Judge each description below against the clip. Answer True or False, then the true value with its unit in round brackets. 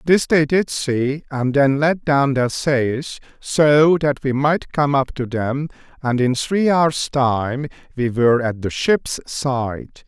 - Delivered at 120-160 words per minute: False (175 wpm)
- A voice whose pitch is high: False (140 Hz)